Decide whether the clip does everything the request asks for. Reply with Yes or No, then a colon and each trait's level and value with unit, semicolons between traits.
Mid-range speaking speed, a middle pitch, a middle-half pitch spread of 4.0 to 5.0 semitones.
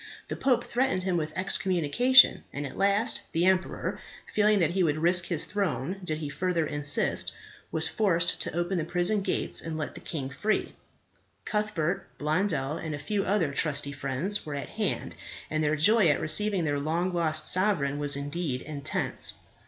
Yes: average, 175 wpm; medium, 170 Hz; average, 4.5 semitones